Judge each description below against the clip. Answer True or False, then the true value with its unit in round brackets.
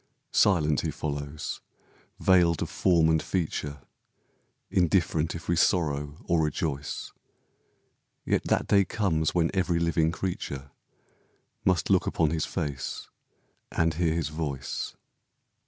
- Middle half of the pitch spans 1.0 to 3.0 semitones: True (2.6 semitones)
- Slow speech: True (120 wpm)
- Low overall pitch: True (80 Hz)